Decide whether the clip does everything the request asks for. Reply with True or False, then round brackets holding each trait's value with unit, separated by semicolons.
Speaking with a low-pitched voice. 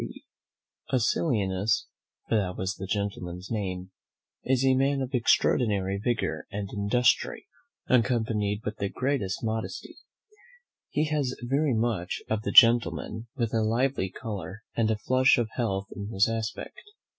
True (110 Hz)